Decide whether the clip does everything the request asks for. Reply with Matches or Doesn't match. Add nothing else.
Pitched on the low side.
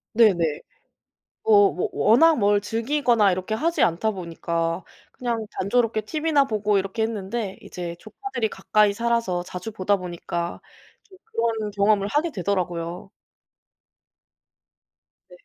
Doesn't match